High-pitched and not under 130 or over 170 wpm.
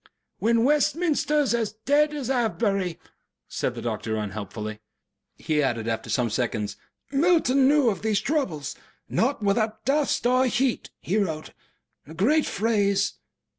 Yes: high, 220 Hz; slow, 135 wpm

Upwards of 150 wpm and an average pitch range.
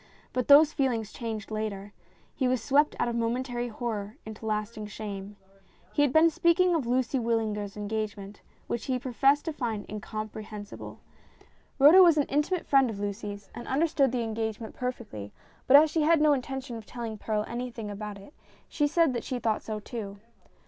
Yes: average, 180 wpm; average, 4.4 semitones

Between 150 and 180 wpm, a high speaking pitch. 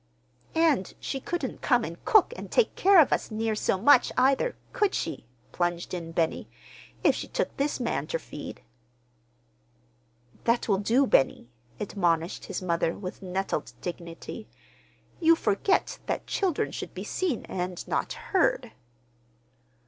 No: average, 140 wpm; high, 225 Hz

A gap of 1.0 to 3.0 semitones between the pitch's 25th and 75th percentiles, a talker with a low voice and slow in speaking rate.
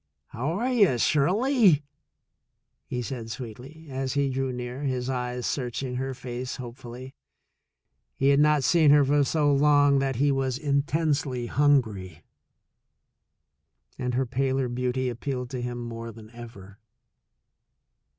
Yes: average, 2.7 semitones; low, 130 Hz; slow, 130 wpm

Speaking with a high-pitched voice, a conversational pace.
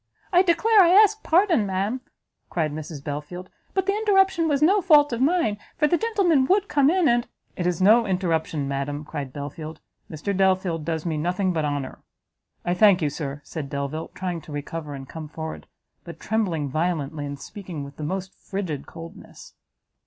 No: medium, 180 Hz; average, 180 wpm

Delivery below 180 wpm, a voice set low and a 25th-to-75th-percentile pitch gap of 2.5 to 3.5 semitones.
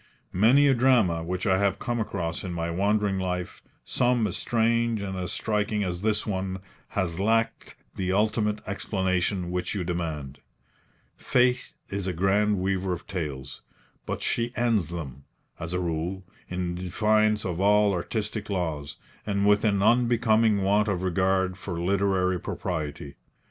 Yes: average, 150 wpm; very low, 95 Hz; average, 3.1 semitones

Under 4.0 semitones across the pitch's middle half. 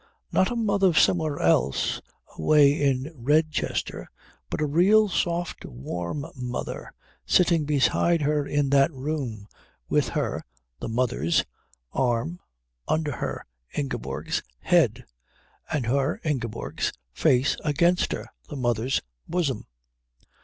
No: average, 4.6 semitones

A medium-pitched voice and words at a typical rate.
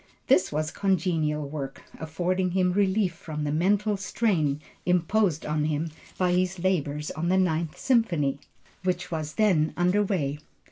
Yes: medium, 175 Hz; average, 145 wpm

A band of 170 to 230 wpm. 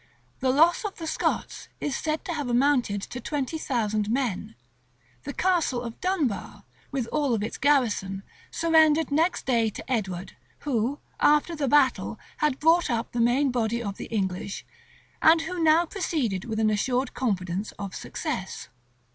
No: average, 155 wpm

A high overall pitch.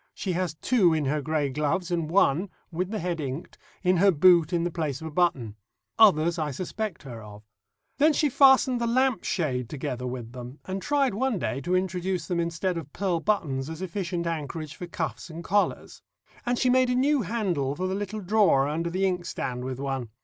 No: medium, 170 Hz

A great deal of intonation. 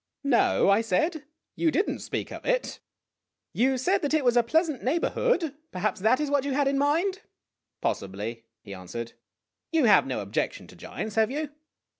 Yes: wide, 6.6 semitones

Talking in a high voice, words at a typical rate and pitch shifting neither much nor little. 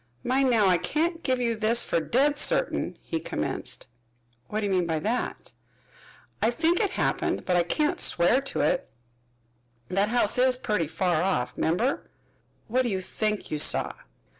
No: high, 225 Hz; average, 170 wpm; wide, 6.3 semitones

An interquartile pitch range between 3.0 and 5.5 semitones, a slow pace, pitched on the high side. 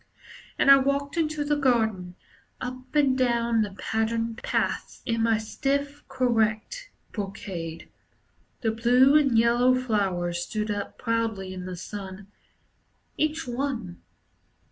Yes: average, 4.5 semitones; slow, 120 wpm; high, 230 Hz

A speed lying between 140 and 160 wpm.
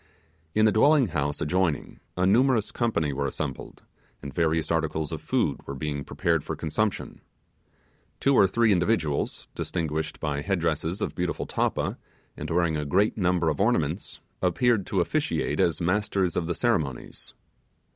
Yes: average, 155 wpm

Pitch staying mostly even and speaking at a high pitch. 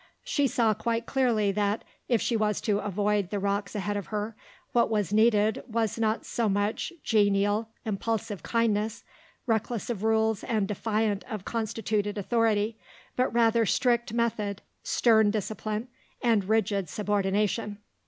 Yes: narrow, 1.9 semitones; high, 215 Hz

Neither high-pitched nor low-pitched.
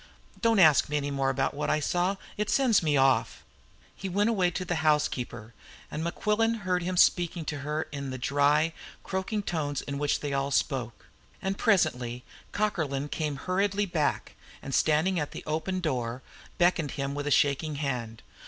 Yes: medium, 150 Hz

